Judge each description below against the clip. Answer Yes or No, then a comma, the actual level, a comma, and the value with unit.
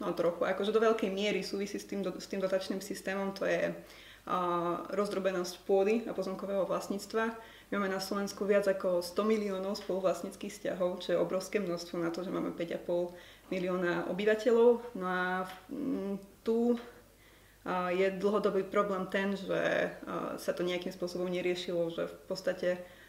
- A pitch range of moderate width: No, narrow, 2.2 semitones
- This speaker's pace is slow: No, average, 160 wpm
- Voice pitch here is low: No, high, 190 Hz